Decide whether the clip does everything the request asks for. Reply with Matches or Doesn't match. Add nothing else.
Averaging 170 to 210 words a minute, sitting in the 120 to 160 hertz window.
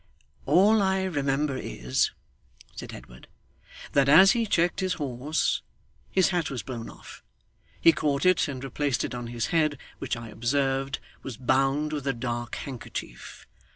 Doesn't match